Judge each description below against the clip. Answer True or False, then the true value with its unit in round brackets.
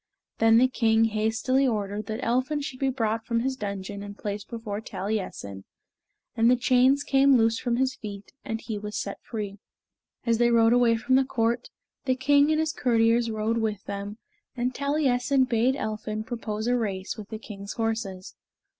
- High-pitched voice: True (225 Hz)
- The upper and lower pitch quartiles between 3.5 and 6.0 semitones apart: False (3.0 semitones)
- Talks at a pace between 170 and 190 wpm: True (180 wpm)